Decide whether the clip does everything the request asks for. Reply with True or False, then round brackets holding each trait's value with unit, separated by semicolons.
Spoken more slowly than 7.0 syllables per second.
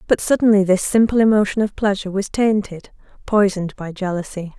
True (5.9 syllables/s)